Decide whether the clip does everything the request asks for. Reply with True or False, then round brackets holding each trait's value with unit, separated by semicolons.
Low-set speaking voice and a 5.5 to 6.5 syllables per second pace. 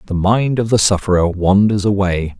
False (100 Hz; 5.0 syllables/s)